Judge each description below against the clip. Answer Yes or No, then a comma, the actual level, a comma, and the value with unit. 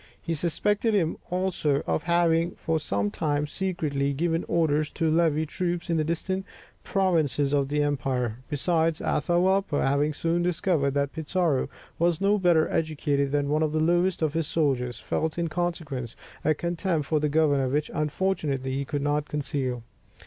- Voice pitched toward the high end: No, medium, 155 Hz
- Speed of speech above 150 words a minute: Yes, average, 165 wpm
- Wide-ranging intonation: No, average, 3.1 semitones